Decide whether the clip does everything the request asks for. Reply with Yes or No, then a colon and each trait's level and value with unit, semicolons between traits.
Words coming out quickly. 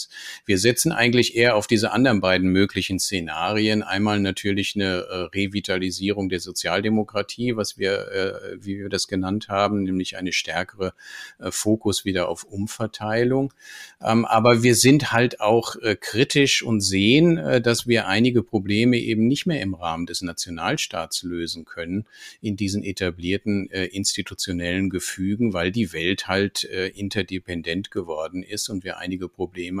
No: average, 150 wpm